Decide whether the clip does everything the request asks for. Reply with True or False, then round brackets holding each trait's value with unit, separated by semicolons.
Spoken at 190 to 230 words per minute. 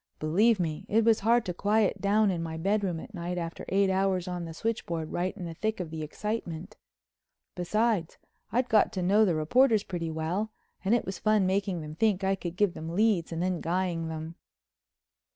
True (200 wpm)